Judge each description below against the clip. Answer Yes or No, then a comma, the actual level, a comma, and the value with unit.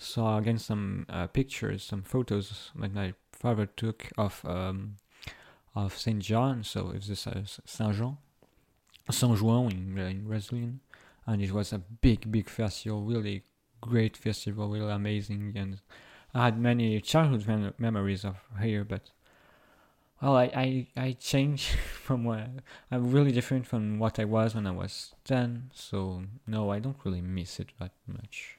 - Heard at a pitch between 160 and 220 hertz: No, low, 110 Hz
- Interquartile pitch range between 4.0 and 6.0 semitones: No, average, 3.4 semitones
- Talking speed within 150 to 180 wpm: Yes, average, 165 wpm